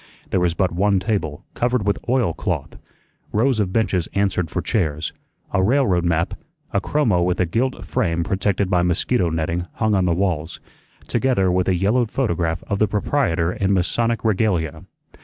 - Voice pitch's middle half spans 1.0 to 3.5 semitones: No, average, 4.2 semitones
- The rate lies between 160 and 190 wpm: Yes, average, 165 wpm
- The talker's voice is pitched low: Yes, very low, 95 Hz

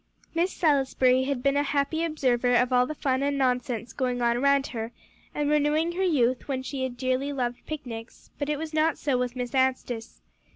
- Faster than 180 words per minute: Yes, average, 200 wpm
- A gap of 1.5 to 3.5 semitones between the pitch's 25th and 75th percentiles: Yes, average, 2.8 semitones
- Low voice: No, very high, 265 Hz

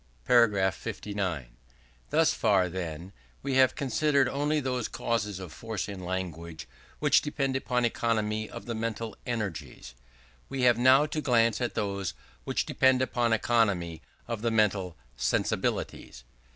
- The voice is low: Yes, low, 110 Hz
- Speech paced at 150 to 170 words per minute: No, average, 140 wpm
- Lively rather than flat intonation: No, average, 4.9 semitones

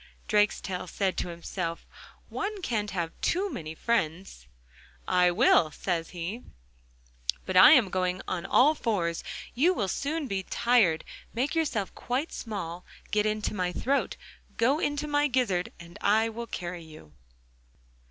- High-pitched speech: Yes, high, 200 Hz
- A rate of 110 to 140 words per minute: Yes, slow, 135 wpm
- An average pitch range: No, wide, 6.1 semitones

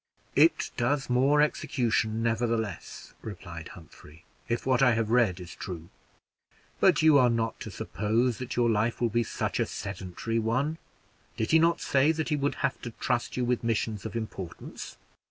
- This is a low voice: Yes, low, 115 Hz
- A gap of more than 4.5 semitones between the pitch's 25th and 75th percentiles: No, average, 3.3 semitones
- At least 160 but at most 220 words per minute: Yes, average, 170 wpm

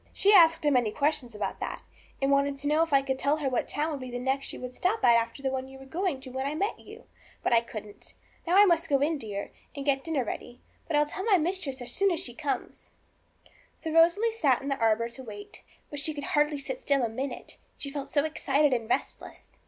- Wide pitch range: No, average, 3.8 semitones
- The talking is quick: Yes, fast, 255 wpm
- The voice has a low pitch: No, very high, 280 Hz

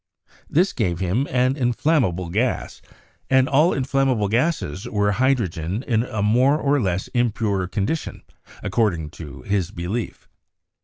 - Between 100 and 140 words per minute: Yes, slow, 135 wpm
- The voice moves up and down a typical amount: No, wide, 5.7 semitones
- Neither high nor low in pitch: No, low, 110 Hz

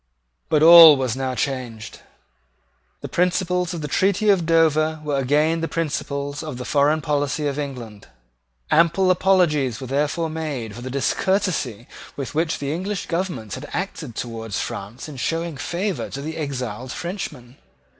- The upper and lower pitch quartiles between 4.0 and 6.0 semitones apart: Yes, average, 4.3 semitones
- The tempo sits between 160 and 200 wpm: No, average, 150 wpm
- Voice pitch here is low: No, medium, 150 Hz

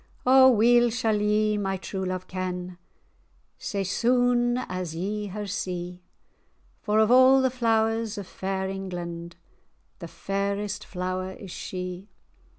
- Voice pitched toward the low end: No, high, 200 Hz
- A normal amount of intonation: Yes, average, 3.4 semitones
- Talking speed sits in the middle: No, slow, 130 wpm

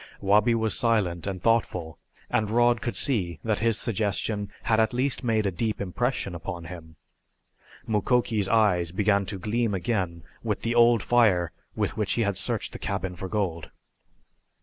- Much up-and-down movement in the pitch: No, average, 3.9 semitones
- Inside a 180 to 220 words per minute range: No, average, 165 wpm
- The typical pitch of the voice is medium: No, low, 105 Hz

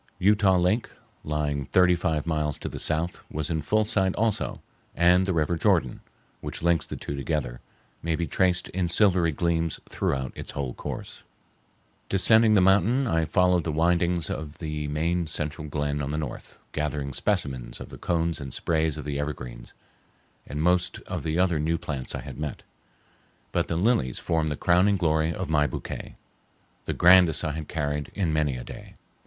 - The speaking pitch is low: Yes, very low, 80 Hz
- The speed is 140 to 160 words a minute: No, average, 175 wpm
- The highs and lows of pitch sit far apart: No, average, 3.3 semitones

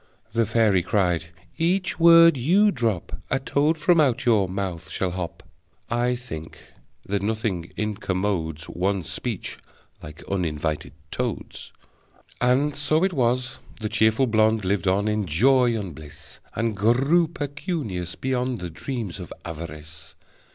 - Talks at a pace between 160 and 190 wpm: No, slow, 135 wpm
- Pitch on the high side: No, low, 110 Hz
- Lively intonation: Yes, wide, 6.6 semitones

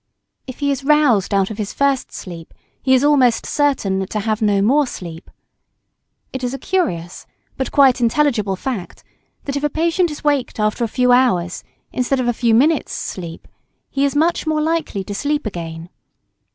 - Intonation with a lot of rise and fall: Yes, wide, 6.2 semitones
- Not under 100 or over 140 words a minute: No, average, 180 wpm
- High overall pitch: Yes, very high, 250 Hz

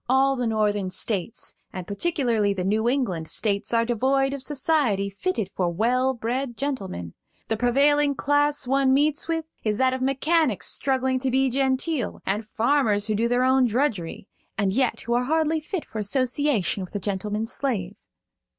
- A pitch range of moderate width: Yes, average, 4.7 semitones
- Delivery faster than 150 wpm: Yes, average, 170 wpm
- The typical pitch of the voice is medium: No, very high, 250 Hz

